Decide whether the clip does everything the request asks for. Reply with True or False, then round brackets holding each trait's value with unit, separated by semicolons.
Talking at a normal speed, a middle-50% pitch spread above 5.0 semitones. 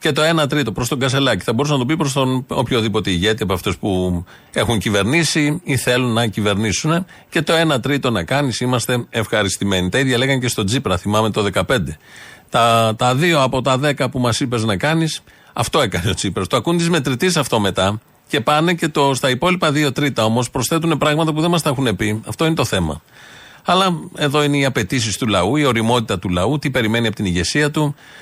False (215 wpm; 5.4 semitones)